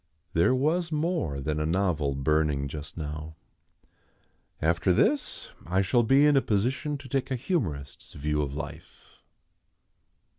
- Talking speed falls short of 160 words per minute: Yes, average, 140 wpm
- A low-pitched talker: Yes, very low, 90 Hz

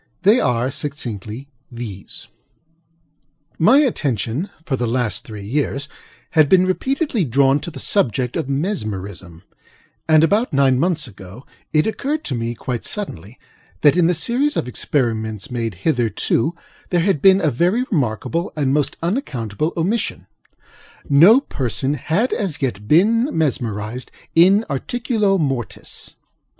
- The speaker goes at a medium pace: No, slow, 130 wpm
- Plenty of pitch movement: Yes, wide, 7.8 semitones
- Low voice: No, medium, 145 Hz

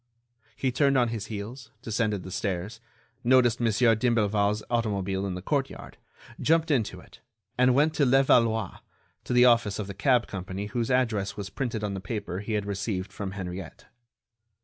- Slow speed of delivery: No, average, 170 wpm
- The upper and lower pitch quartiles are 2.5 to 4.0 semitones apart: Yes, average, 3.7 semitones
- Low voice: Yes, low, 110 Hz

